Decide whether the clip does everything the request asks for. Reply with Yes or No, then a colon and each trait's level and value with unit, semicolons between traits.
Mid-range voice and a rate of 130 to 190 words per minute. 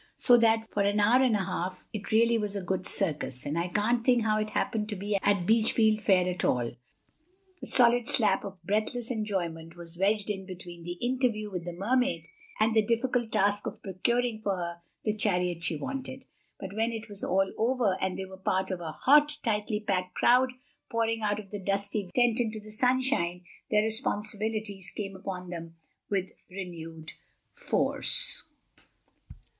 No: high, 205 Hz; average, 175 wpm